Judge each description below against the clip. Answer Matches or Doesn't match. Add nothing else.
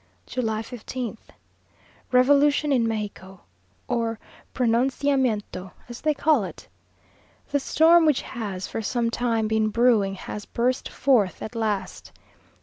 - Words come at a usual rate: Doesn't match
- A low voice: Doesn't match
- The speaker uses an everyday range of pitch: Matches